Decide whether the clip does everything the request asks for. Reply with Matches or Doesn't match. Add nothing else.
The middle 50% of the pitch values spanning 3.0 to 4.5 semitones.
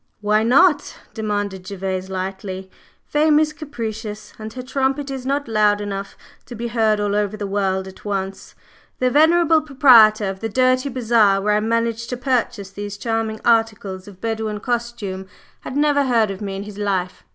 Matches